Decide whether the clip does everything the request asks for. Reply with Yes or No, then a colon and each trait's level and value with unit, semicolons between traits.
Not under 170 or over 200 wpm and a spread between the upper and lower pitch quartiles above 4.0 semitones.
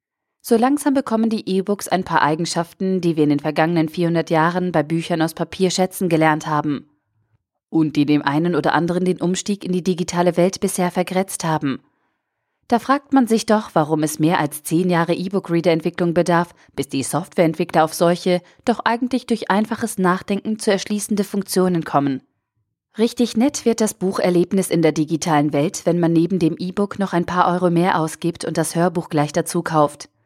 No: average, 180 wpm; average, 3.4 semitones